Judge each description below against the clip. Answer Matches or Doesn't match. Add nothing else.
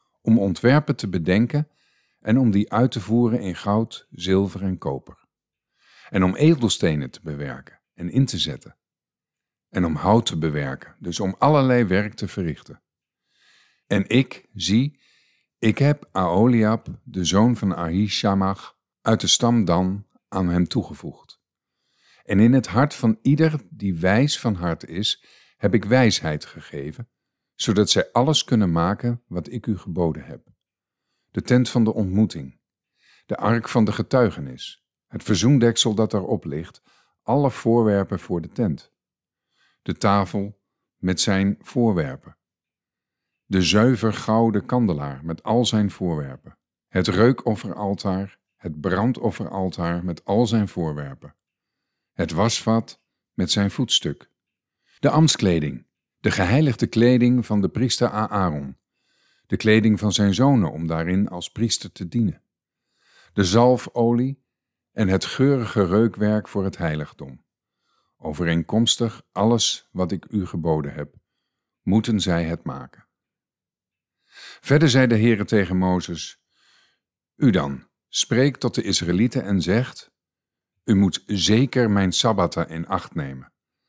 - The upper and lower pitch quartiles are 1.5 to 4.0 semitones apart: Doesn't match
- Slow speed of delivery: Matches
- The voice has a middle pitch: Doesn't match